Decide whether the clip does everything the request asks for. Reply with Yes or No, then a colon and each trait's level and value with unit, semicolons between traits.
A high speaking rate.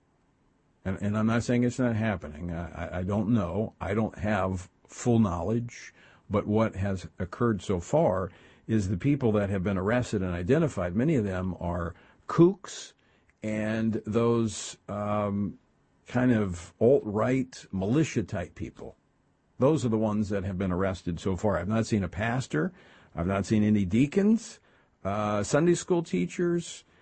No: average, 160 wpm